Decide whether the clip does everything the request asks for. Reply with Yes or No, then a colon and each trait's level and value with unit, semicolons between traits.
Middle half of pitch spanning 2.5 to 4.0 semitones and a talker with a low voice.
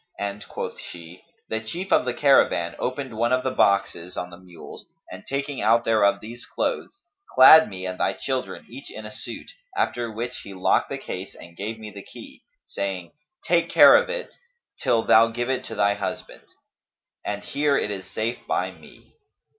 No: average, 4.6 semitones; low, 110 Hz